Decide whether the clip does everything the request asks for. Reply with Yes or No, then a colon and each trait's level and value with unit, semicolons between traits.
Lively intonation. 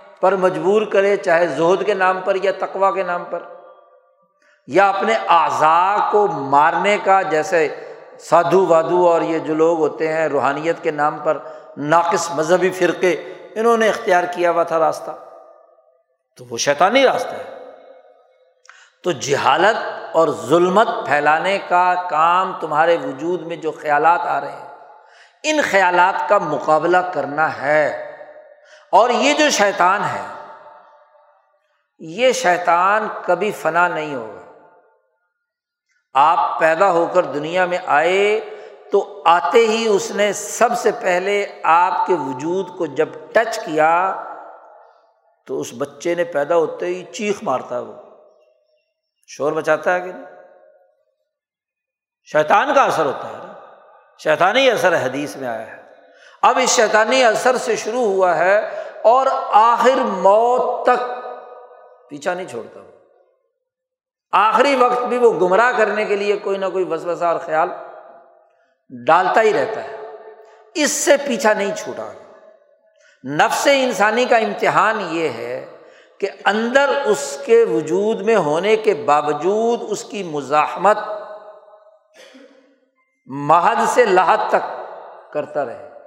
Yes: wide, 7.3 semitones